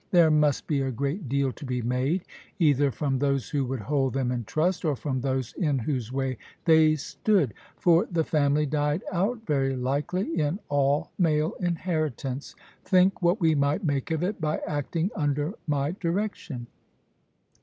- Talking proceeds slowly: No, average, 165 wpm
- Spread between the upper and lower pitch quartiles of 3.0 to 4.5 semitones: Yes, average, 3.7 semitones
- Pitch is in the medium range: Yes, medium, 145 Hz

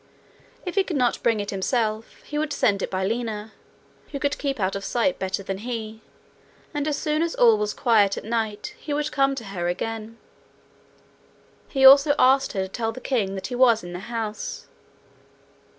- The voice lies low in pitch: No, high, 230 Hz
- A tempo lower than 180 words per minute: No, average, 195 wpm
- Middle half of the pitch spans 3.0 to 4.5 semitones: No, average, 4.9 semitones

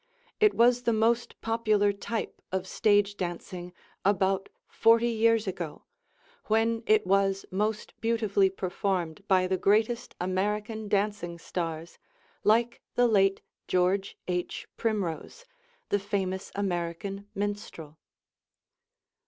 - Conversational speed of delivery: No, slow, 110 wpm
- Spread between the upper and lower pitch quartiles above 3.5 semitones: No, average, 2.9 semitones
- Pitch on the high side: Yes, high, 200 Hz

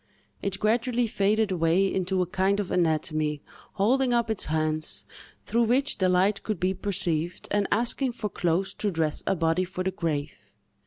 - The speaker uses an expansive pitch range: No, average, 4.3 semitones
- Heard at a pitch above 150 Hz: Yes, high, 190 Hz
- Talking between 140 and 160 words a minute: No, average, 170 wpm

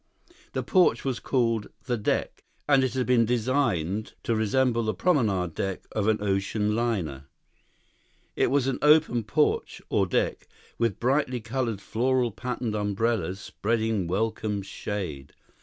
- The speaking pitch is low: Yes, low, 115 Hz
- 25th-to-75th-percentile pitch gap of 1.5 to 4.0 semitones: Yes, average, 3.7 semitones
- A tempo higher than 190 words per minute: No, average, 140 wpm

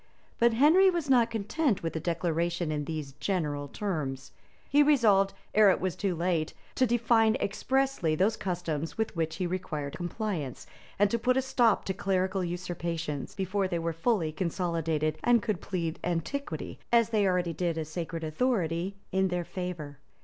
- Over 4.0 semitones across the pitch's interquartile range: Yes, average, 5.0 semitones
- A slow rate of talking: No, average, 165 wpm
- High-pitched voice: No, medium, 180 Hz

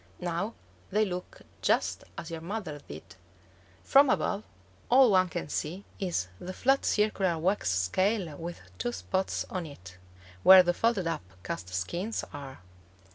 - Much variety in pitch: Yes, wide, 5.7 semitones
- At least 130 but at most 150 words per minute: Yes, average, 145 wpm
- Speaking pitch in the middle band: Yes, medium, 180 Hz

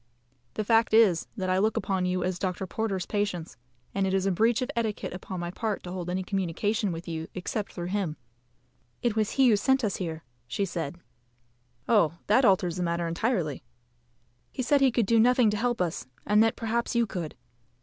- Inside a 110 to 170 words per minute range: No, average, 200 wpm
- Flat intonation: No, average, 4.0 semitones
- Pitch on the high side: Yes, high, 195 Hz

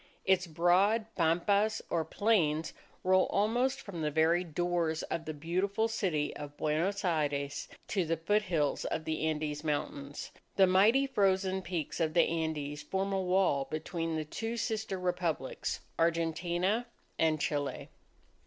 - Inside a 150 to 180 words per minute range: No, average, 140 wpm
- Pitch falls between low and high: Yes, medium, 170 Hz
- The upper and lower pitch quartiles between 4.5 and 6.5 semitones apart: No, average, 3.8 semitones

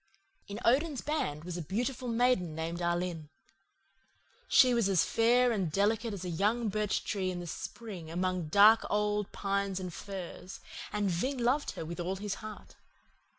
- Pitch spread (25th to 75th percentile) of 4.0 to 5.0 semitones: Yes, average, 4.4 semitones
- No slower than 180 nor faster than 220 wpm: No, average, 165 wpm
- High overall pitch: Yes, high, 200 Hz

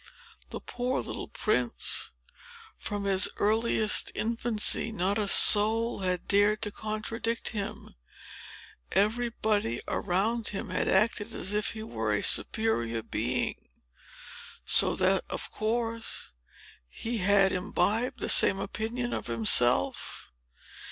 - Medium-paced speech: No, slow, 115 wpm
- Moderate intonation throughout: Yes, average, 3.1 semitones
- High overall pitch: Yes, high, 210 Hz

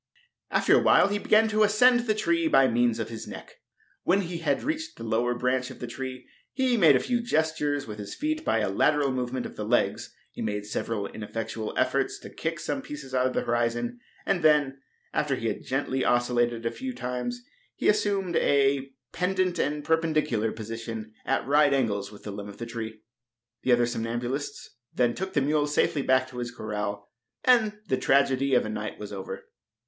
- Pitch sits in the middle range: No, low, 130 Hz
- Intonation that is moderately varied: No, wide, 5.9 semitones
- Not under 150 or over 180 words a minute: No, average, 195 wpm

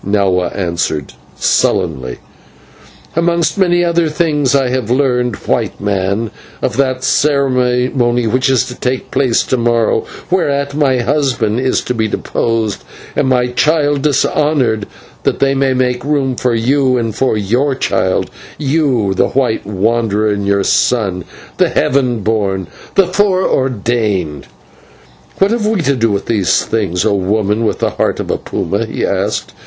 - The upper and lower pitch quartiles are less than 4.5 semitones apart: No, average, 4.8 semitones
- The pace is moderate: Yes, average, 150 wpm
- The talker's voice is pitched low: Yes, low, 125 Hz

